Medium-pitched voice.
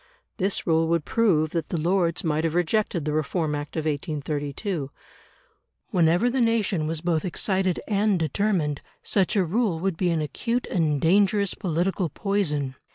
Yes: medium, 170 Hz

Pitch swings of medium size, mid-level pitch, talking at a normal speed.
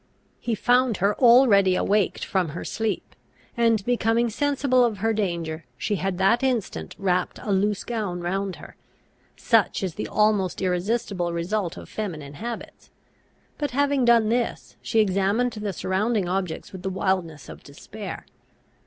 No: average, 4.1 semitones; high, 205 Hz; average, 150 wpm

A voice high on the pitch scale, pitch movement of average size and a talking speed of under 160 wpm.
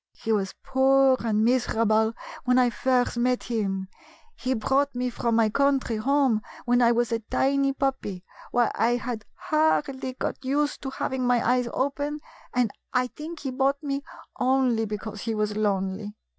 No: very high, 250 Hz; average, 3.4 semitones; average, 165 wpm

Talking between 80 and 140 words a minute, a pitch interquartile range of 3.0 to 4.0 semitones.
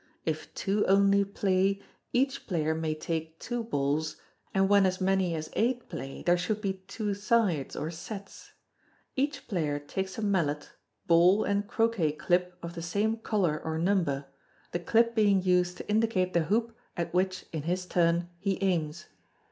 No: average, 165 wpm; average, 3.7 semitones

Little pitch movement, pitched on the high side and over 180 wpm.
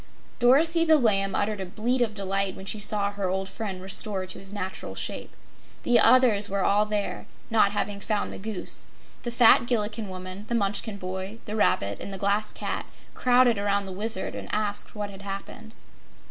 Yes: narrow, 2.2 semitones; high, 205 Hz; average, 190 wpm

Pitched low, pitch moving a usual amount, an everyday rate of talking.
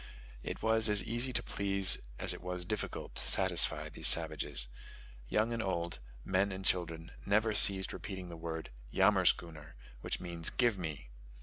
Yes: very low, 95 Hz; average, 3.6 semitones; average, 160 wpm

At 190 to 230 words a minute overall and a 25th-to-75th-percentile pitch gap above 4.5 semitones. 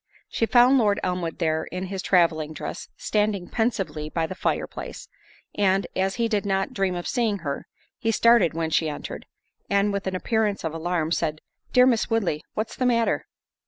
No: average, 180 wpm; average, 5.0 semitones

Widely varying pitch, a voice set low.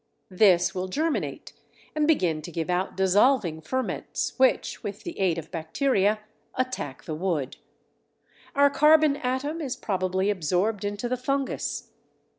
No: wide, 6.9 semitones; high, 205 Hz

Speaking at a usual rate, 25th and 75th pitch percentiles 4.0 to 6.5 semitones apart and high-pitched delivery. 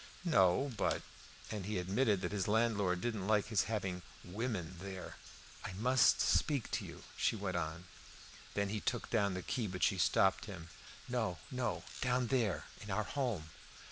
No: average, 175 wpm; average, 4.3 semitones; low, 100 Hz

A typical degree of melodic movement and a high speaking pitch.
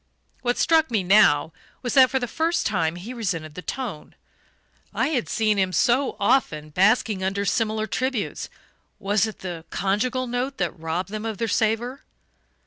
Yes: average, 5.0 semitones; high, 215 Hz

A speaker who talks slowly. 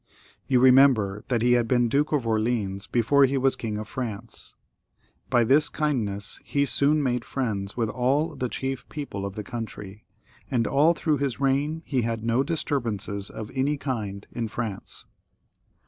No: average, 165 wpm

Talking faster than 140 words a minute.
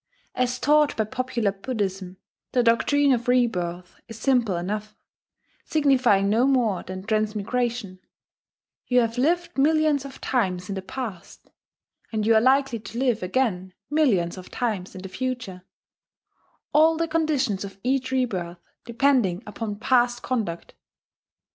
No: slow, 135 wpm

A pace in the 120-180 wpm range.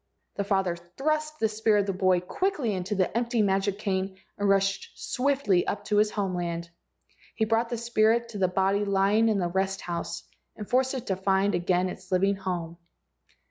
No: average, 190 wpm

